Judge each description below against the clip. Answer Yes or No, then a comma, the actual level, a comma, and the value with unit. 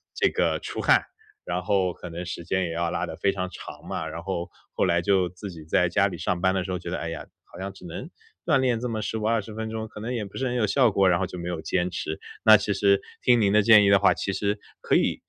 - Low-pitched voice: Yes, very low, 95 Hz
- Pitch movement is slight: No, average, 3.5 semitones